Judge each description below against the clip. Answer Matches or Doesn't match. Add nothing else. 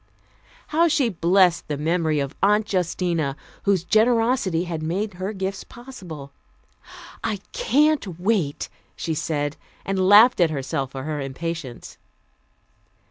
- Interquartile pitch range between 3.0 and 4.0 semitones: Doesn't match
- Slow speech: Matches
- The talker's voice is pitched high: Doesn't match